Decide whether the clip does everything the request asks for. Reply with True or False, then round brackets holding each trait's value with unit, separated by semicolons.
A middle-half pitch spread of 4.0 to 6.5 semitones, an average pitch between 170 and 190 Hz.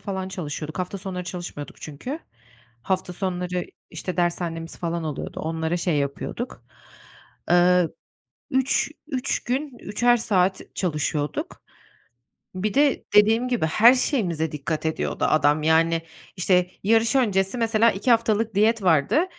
True (5.6 semitones; 185 Hz)